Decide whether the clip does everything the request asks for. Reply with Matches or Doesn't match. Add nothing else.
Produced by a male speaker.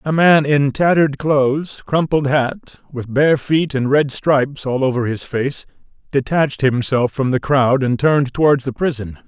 Matches